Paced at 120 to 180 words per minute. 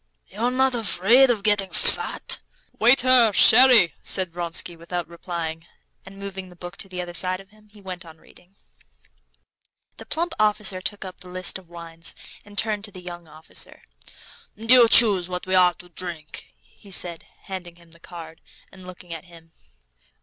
Yes: average, 170 wpm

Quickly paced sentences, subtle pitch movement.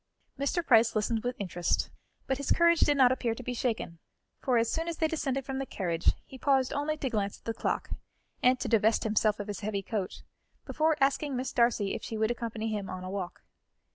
No: fast, 220 wpm; average, 4.3 semitones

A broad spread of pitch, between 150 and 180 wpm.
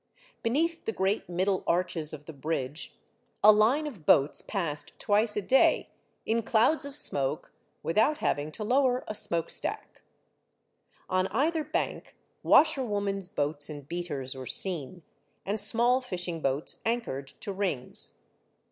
No: wide, 7.1 semitones; average, 140 wpm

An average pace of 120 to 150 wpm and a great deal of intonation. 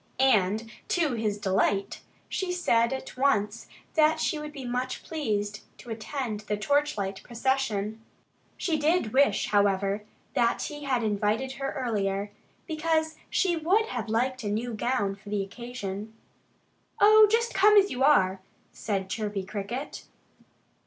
Yes: average, 140 wpm; wide, 5.8 semitones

